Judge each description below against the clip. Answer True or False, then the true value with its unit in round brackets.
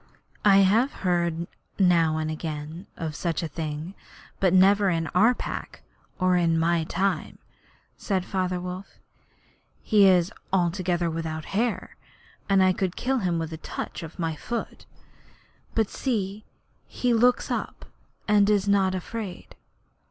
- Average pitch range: True (3.3 semitones)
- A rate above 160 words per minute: False (140 wpm)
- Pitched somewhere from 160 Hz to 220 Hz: True (185 Hz)